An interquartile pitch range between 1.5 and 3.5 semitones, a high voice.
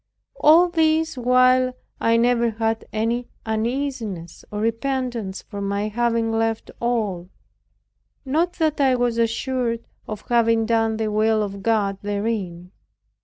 Yes: average, 2.8 semitones; high, 230 Hz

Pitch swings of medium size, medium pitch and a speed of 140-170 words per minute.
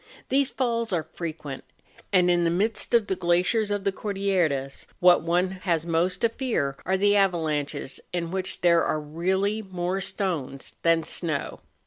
Yes: average, 3.2 semitones; medium, 180 Hz; average, 160 wpm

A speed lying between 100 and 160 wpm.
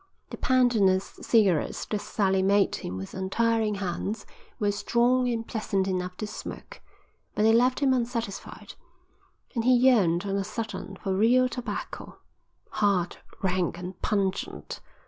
Yes: average, 145 wpm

